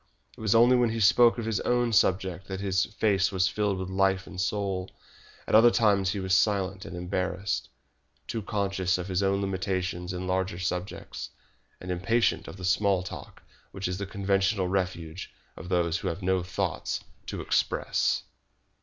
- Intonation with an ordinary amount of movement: No, narrow, 1.7 semitones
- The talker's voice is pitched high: No, very low, 95 Hz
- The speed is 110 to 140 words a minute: No, average, 175 wpm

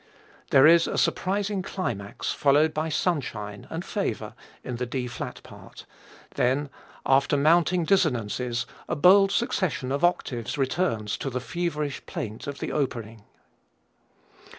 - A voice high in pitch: No, medium, 140 Hz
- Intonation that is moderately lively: No, wide, 5.8 semitones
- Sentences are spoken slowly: Yes, slow, 130 wpm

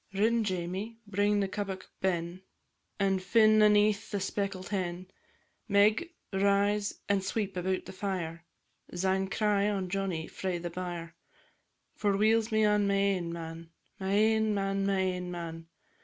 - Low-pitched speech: No, high, 195 Hz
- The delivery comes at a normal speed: Yes, average, 145 wpm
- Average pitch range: No, narrow, 2.1 semitones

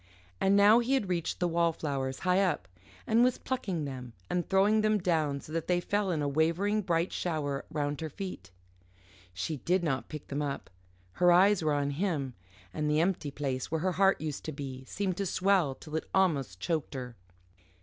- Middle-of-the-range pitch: Yes, medium, 165 Hz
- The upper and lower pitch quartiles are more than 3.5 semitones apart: Yes, average, 5.0 semitones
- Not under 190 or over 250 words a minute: Yes, average, 195 wpm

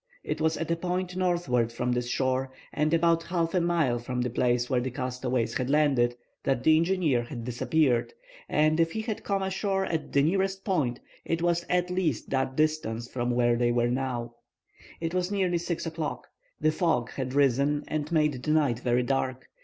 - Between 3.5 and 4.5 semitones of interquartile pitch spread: No, wide, 5.5 semitones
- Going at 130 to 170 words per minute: No, average, 195 wpm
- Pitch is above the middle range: No, medium, 150 Hz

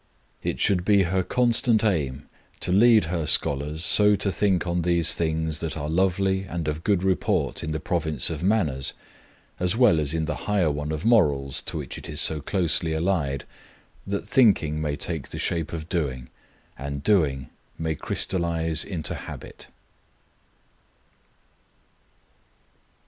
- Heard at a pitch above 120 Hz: No, very low, 85 Hz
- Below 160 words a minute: Yes, average, 150 wpm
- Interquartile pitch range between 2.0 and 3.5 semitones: No, average, 4.0 semitones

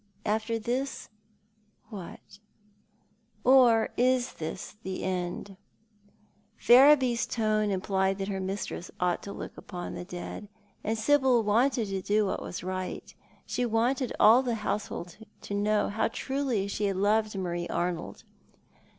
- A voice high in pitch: Yes, high, 210 Hz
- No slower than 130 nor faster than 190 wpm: Yes, slow, 135 wpm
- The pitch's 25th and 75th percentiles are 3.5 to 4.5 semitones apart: Yes, average, 3.9 semitones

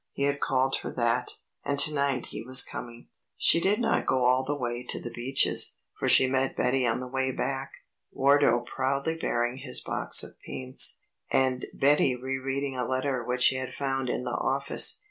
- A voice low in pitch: Yes, low, 130 Hz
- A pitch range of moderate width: No, narrow, 1.6 semitones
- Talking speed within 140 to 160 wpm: No, average, 195 wpm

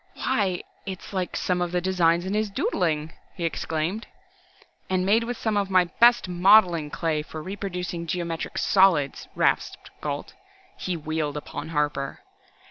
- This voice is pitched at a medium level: Yes, medium, 180 Hz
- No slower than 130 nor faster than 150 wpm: Yes, average, 145 wpm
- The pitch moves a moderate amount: Yes, average, 3.2 semitones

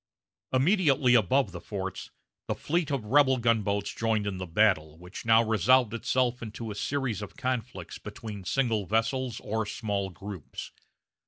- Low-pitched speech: Yes, low, 110 Hz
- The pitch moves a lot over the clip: No, average, 4.1 semitones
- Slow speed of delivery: No, average, 150 wpm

